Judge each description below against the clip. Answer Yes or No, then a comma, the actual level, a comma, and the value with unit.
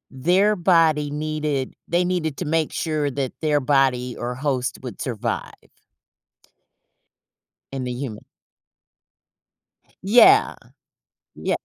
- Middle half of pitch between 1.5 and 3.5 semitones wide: No, average, 4.2 semitones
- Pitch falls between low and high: Yes, medium, 150 Hz